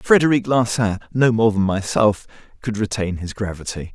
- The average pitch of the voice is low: Yes, low, 110 Hz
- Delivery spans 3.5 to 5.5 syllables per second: Yes, 5.0 syllables/s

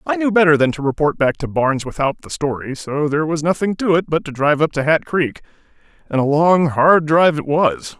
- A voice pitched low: No, medium, 155 Hz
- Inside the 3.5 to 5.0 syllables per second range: No, 5.8 syllables/s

